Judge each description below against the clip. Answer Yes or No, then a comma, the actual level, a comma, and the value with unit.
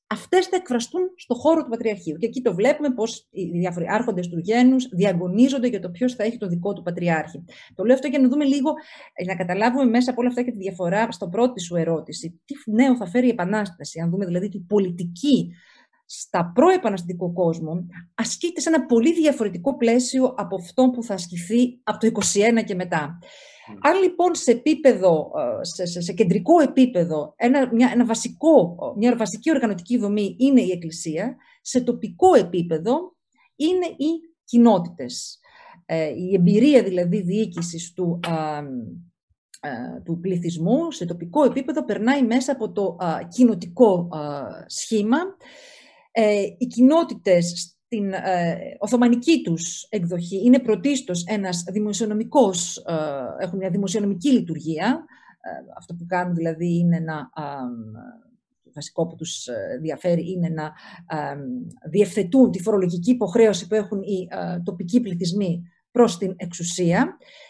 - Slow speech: No, average, 150 wpm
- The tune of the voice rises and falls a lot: Yes, wide, 6.2 semitones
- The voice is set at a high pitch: Yes, high, 210 Hz